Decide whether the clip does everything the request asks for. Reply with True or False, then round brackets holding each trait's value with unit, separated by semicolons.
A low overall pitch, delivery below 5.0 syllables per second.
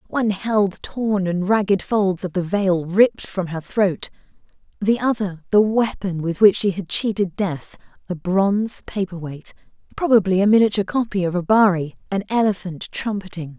False (195 Hz; 4.8 syllables/s)